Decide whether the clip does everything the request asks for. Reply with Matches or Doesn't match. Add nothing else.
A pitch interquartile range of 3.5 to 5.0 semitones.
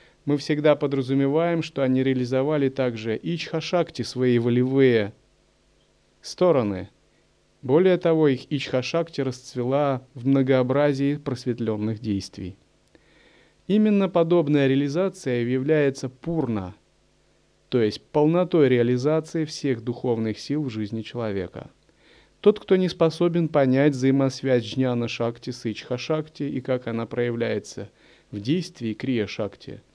Matches